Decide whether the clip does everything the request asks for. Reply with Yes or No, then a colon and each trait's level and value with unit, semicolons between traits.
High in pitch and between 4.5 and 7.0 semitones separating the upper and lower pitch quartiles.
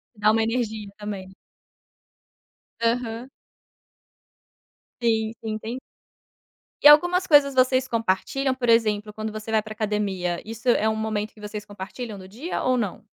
No: high, 220 Hz; average, 2.8 semitones